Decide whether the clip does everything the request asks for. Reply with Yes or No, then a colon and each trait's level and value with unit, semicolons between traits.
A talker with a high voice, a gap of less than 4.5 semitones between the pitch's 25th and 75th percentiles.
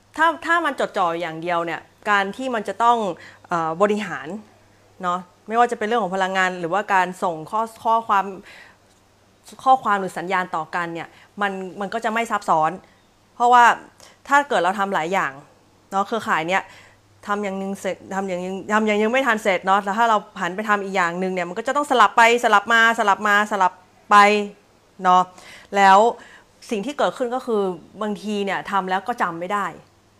Yes: high, 200 Hz; average, 3.5 semitones